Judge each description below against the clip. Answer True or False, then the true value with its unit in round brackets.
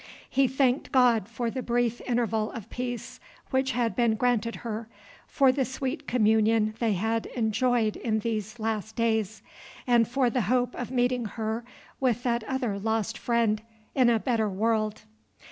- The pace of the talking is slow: False (160 wpm)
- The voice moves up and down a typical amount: False (2.1 semitones)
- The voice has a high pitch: True (230 Hz)